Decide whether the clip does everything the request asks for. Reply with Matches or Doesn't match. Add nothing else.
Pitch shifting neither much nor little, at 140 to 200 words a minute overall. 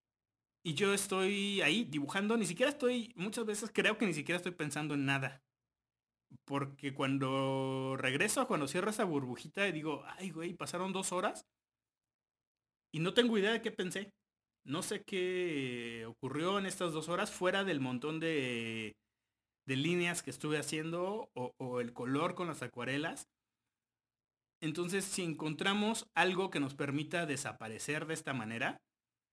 Doesn't match